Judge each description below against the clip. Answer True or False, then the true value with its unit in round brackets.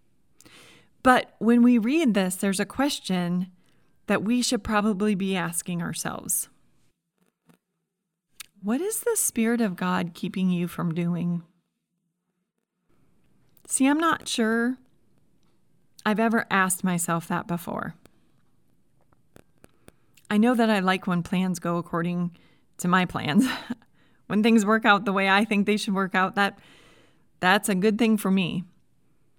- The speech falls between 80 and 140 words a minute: True (135 wpm)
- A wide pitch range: False (3.9 semitones)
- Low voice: False (195 Hz)